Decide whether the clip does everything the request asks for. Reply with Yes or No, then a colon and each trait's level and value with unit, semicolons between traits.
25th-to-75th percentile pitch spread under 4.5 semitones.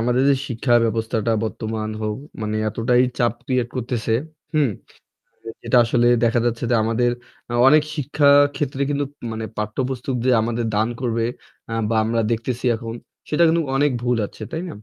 Yes: narrow, 2.5 semitones